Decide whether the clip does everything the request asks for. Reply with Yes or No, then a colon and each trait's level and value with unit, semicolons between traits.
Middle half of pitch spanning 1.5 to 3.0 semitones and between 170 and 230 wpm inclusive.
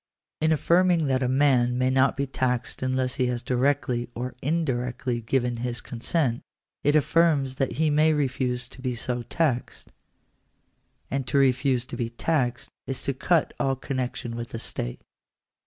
No: narrow, 2.4 semitones; average, 160 wpm